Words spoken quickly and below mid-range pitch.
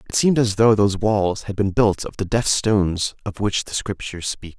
Yes: fast, 235 wpm; low, 100 Hz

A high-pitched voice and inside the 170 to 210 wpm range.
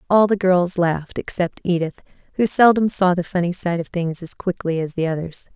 No: medium, 180 Hz; fast, 205 wpm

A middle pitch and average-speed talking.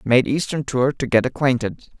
No: low, 130 Hz; average, 180 wpm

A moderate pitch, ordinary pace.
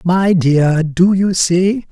Yes: medium, 180 Hz; average, 155 wpm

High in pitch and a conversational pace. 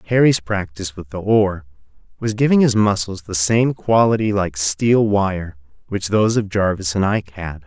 No: low, 100 Hz; average, 170 wpm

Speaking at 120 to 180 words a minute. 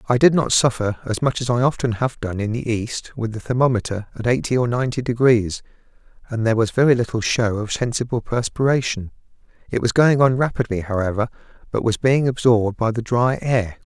No: average, 195 wpm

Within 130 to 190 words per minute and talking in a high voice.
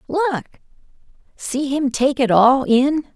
Yes: slow, 135 wpm; very high, 270 Hz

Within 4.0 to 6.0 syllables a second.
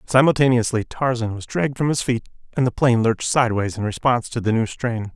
No: 6.3 syllables/s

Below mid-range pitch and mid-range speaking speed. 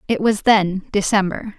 No: high, 205 Hz; average, 150 wpm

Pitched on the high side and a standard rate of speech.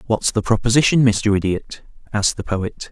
No: low, 110 Hz; average, 165 wpm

